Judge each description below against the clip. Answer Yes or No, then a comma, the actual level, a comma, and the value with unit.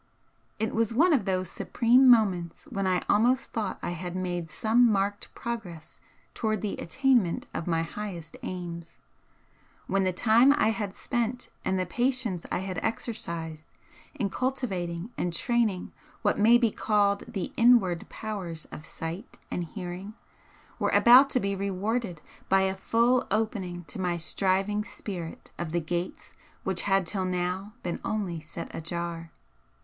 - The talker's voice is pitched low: No, high, 195 Hz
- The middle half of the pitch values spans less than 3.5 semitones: No, average, 4.3 semitones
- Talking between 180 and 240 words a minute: No, average, 150 wpm